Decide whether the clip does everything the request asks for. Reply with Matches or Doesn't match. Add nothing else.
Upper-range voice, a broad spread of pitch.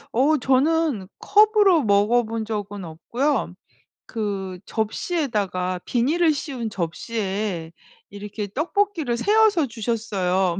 Matches